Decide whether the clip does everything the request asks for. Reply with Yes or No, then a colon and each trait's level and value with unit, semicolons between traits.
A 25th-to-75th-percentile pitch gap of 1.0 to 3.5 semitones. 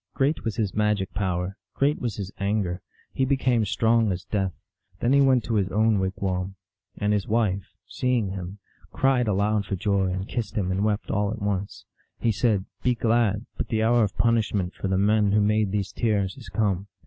Yes: average, 2.8 semitones